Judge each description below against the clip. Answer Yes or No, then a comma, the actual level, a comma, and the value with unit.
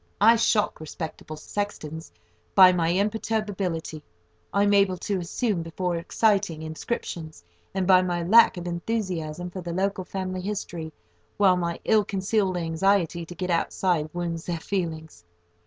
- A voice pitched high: No, medium, 180 Hz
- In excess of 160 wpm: No, average, 140 wpm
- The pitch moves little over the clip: No, average, 3.1 semitones